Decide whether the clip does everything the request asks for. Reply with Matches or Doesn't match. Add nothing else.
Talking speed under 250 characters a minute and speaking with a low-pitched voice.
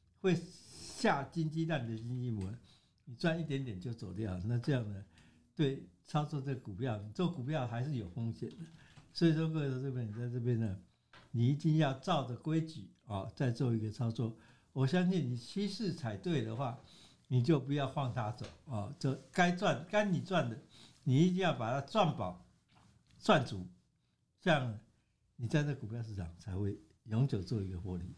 Doesn't match